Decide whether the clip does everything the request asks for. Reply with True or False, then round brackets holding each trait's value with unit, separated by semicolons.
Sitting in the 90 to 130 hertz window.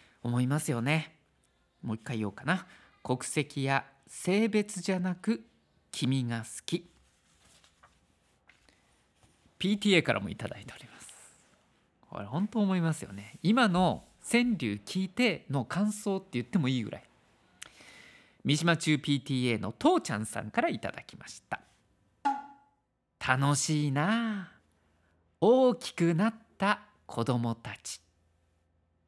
False (140 Hz)